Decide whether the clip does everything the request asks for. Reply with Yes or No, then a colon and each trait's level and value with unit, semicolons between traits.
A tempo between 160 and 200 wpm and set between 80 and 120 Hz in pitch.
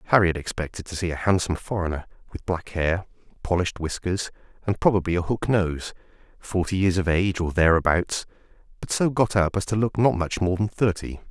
Yes: average, 185 wpm; very low, 90 Hz